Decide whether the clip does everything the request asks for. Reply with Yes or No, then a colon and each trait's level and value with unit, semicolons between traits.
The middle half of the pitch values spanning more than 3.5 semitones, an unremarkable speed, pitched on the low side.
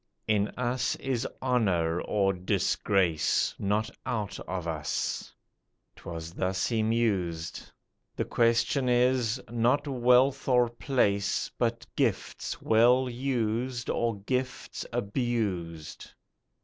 No: average, 4.2 semitones; slow, 100 wpm; low, 115 Hz